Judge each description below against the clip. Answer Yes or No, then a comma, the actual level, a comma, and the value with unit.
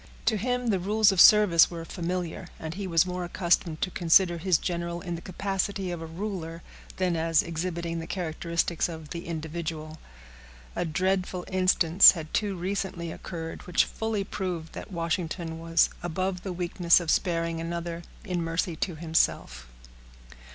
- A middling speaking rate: Yes, average, 160 wpm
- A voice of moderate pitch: Yes, medium, 170 Hz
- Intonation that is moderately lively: No, narrow, 2.1 semitones